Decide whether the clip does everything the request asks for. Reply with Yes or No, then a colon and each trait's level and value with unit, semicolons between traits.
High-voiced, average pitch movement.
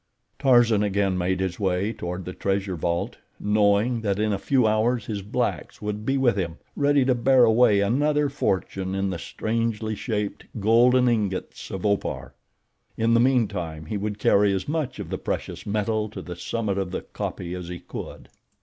No: low, 105 Hz; average, 3.5 semitones